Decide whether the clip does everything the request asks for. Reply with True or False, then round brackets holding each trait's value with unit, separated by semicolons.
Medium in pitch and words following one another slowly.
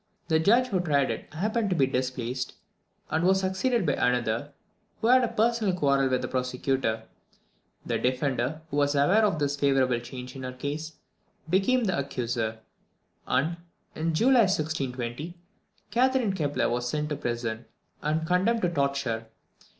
False (145 Hz; 160 wpm)